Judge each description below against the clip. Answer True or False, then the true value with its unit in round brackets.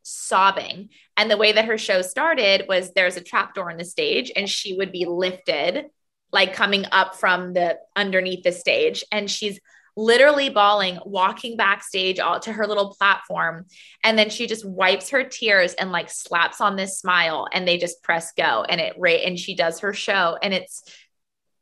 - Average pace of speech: True (190 wpm)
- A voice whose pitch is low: False (195 Hz)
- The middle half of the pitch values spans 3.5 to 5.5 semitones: False (2.7 semitones)